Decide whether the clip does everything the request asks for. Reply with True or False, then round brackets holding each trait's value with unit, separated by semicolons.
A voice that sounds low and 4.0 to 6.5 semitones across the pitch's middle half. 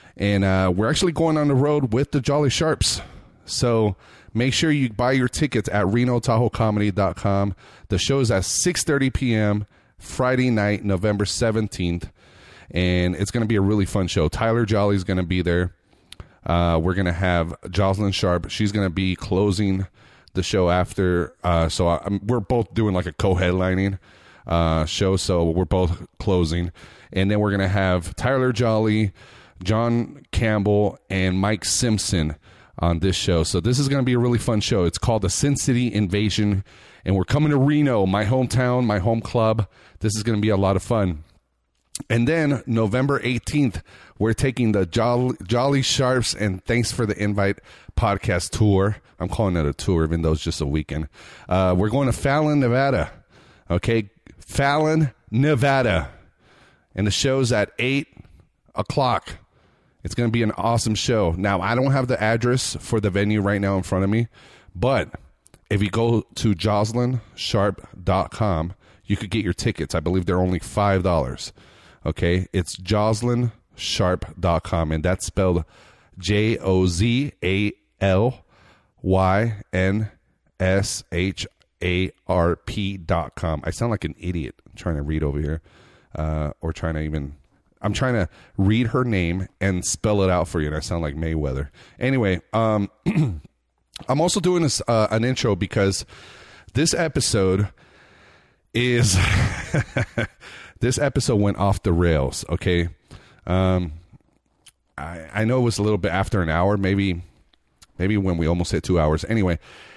True (100 Hz; 4.6 semitones)